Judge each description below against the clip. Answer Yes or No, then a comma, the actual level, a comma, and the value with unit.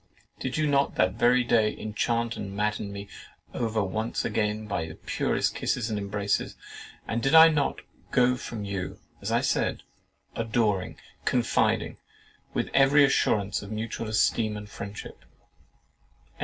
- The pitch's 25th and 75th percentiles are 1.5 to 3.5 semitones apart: Yes, average, 3.0 semitones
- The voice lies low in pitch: Yes, low, 110 Hz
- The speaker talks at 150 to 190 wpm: No, average, 140 wpm